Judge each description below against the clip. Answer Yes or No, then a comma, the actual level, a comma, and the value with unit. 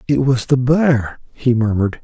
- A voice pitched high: No, low, 125 Hz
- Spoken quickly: No, average, 175 wpm